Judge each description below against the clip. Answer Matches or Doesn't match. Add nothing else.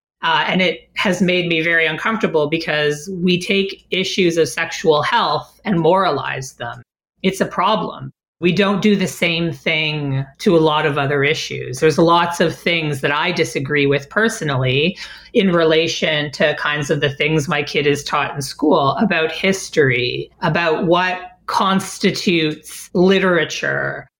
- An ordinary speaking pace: Matches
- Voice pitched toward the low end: Doesn't match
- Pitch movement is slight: Doesn't match